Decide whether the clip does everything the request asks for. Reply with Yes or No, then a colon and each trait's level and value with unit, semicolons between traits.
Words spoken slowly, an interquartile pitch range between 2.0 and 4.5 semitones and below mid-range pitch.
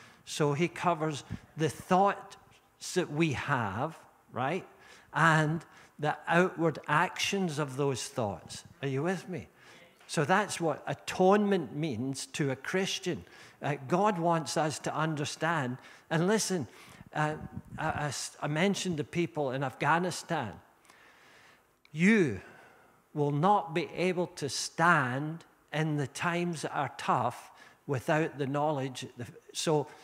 No: slow, 125 wpm; average, 3.5 semitones; medium, 155 Hz